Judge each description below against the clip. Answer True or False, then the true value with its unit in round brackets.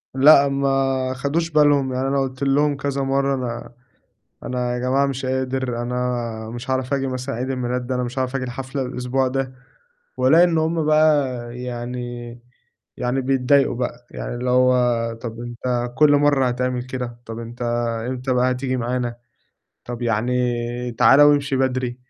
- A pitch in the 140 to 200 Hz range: False (130 Hz)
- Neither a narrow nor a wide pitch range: False (1.7 semitones)